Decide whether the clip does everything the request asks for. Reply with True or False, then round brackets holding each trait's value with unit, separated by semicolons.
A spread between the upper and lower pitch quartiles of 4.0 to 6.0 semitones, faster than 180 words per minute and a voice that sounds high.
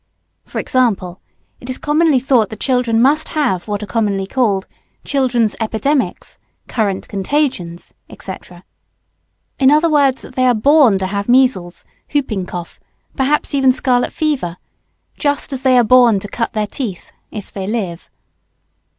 False (5.1 semitones; 150 wpm; 245 Hz)